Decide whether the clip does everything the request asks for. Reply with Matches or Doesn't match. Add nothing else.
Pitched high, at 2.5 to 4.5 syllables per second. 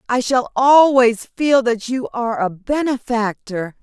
Matches